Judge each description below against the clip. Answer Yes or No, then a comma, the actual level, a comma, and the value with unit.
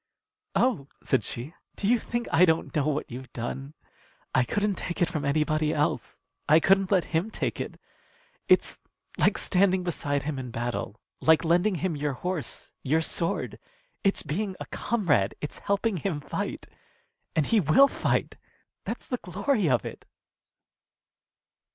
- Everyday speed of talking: Yes, average, 155 wpm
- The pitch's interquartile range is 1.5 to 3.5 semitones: No, average, 5.2 semitones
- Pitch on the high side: No, medium, 160 Hz